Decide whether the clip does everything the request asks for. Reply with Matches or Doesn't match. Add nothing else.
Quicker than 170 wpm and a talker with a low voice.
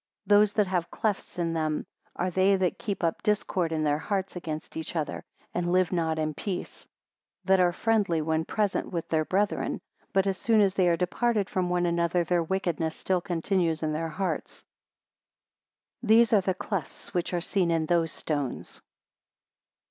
Doesn't match